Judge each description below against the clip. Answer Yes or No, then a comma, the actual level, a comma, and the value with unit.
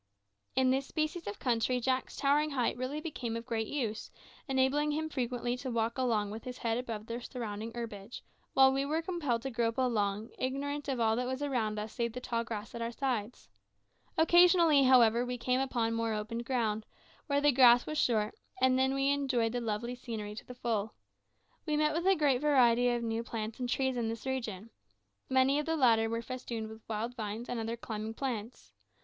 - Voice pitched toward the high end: Yes, high, 245 Hz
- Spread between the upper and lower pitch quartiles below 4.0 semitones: Yes, average, 2.9 semitones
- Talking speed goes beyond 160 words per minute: Yes, average, 200 wpm